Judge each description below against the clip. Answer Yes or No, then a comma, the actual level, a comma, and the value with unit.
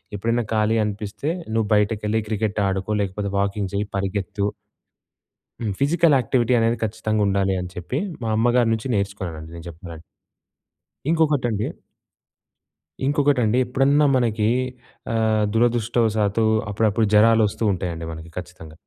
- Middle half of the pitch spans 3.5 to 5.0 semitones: No, average, 2.8 semitones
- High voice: No, low, 105 Hz